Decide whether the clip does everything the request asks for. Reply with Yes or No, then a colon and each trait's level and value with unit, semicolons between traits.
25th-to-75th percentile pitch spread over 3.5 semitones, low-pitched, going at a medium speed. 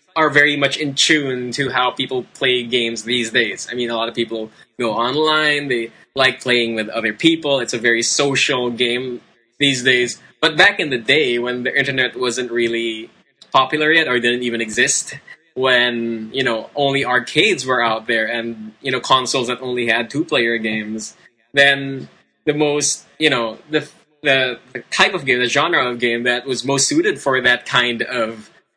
No: average, 3.1 semitones; low, 125 Hz; average, 190 wpm